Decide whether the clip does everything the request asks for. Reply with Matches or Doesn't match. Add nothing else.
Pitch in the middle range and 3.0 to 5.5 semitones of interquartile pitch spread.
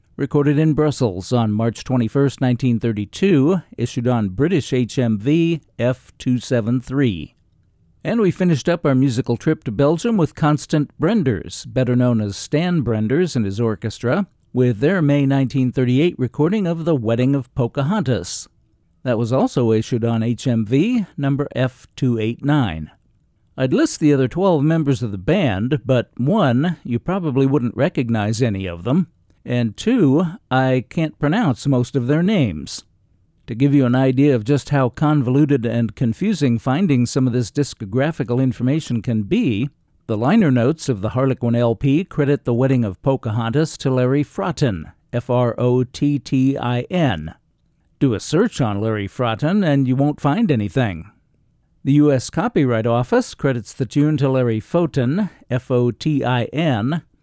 Doesn't match